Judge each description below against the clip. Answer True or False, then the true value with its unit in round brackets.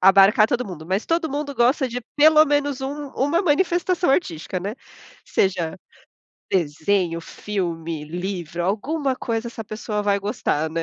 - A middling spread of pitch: False (8.1 semitones)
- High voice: True (210 Hz)